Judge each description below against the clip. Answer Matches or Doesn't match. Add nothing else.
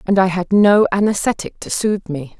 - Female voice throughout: Matches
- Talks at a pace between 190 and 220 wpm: Matches